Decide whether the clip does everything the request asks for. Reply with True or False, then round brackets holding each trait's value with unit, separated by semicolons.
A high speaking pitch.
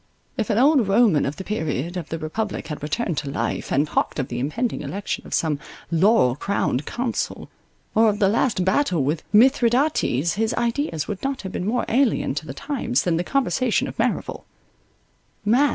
True (200 Hz)